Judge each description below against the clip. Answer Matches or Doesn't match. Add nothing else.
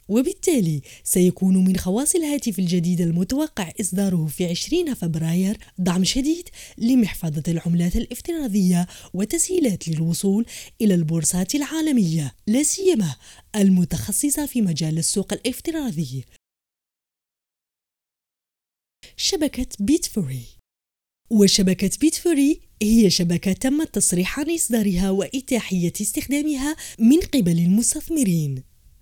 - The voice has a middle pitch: Doesn't match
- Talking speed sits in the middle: Matches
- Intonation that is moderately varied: Doesn't match